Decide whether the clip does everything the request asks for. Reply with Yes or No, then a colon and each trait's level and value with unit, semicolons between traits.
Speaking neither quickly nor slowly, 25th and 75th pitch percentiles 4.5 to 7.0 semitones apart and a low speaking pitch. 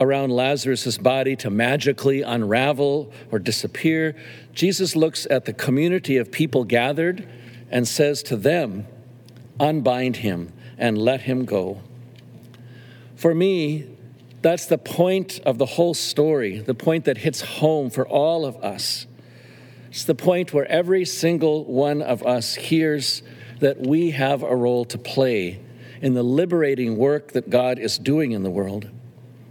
No: average, 145 wpm; average, 3.8 semitones; low, 130 Hz